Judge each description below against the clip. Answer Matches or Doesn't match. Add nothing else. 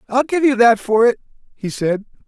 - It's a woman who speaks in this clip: Doesn't match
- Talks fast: Matches